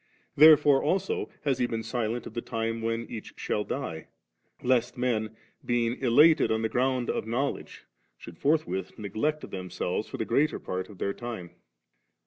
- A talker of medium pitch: No, low, 120 Hz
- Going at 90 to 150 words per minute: No, average, 160 wpm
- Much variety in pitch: No, average, 3.7 semitones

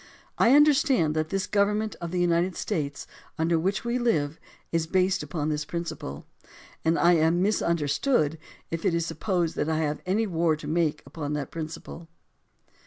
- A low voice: No, medium, 165 Hz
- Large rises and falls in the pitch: No, average, 3.5 semitones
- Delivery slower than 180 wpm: Yes, average, 170 wpm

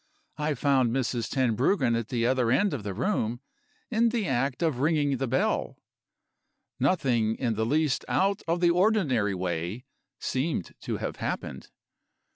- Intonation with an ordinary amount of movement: No, wide, 5.7 semitones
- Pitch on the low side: Yes, low, 130 Hz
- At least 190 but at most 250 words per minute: No, average, 150 wpm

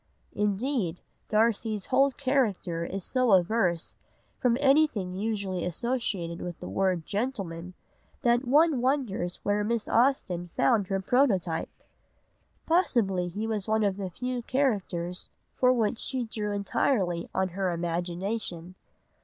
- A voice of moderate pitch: No, high, 205 Hz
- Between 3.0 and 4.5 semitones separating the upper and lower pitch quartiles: No, wide, 5.4 semitones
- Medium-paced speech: No, slow, 130 wpm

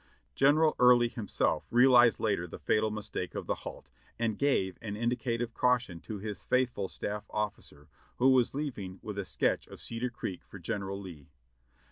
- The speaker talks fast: No, average, 165 wpm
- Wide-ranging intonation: No, average, 3.9 semitones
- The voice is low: Yes, low, 110 Hz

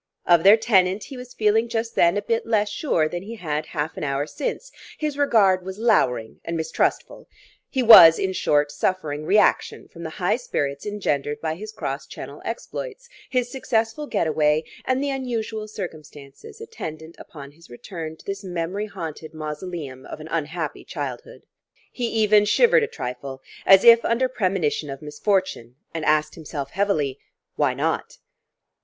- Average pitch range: No, wide, 6.6 semitones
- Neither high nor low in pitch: Yes, medium, 180 Hz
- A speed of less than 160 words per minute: No, average, 165 wpm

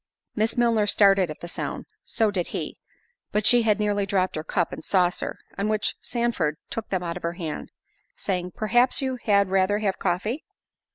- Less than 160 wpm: No, average, 175 wpm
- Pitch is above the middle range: Yes, high, 200 Hz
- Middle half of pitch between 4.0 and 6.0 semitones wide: No, average, 3.5 semitones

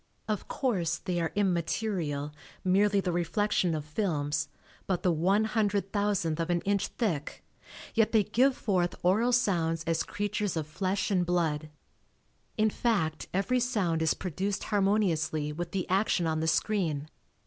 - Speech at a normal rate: Yes, average, 150 wpm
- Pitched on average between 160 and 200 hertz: Yes, medium, 185 Hz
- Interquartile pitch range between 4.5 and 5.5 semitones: No, average, 4.1 semitones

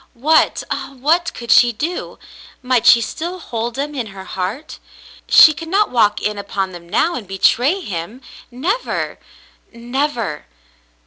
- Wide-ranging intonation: Yes, wide, 6.8 semitones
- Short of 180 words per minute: Yes, average, 165 wpm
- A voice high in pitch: Yes, high, 245 Hz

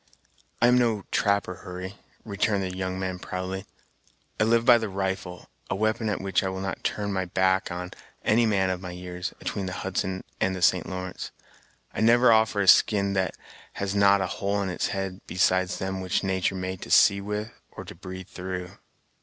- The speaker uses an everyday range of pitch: No, narrow, 1.6 semitones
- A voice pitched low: Yes, very low, 95 Hz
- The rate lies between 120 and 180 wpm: No, average, 195 wpm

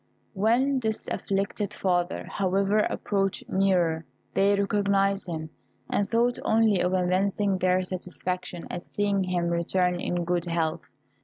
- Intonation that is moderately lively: No, narrow, 2.1 semitones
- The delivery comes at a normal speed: No, slow, 130 wpm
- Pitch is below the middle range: No, high, 190 Hz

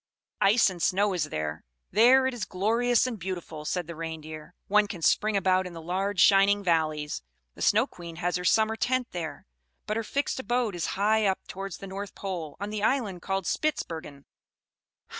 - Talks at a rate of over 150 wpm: Yes, average, 185 wpm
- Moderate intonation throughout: Yes, average, 4.1 semitones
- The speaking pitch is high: Yes, high, 195 Hz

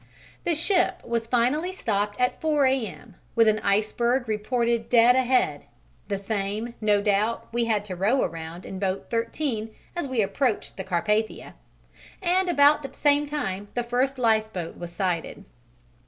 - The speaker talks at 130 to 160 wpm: Yes, average, 155 wpm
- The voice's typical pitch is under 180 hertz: No, high, 230 Hz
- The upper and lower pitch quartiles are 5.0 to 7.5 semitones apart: No, average, 4.3 semitones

